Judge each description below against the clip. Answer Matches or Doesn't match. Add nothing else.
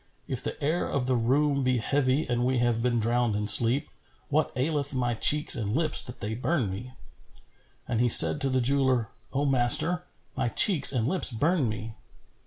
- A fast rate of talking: Doesn't match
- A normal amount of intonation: Matches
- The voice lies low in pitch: Matches